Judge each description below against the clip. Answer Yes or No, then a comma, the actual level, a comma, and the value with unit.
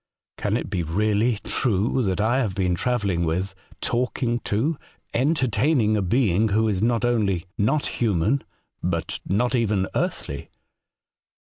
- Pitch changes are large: No, average, 4.3 semitones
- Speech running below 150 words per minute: Yes, average, 140 wpm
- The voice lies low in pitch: Yes, low, 110 Hz